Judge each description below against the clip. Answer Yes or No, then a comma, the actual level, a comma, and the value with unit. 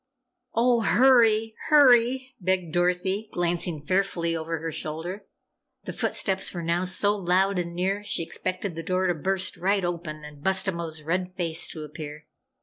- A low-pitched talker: No, medium, 180 Hz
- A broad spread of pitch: No, average, 2.9 semitones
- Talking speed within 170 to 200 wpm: No, average, 150 wpm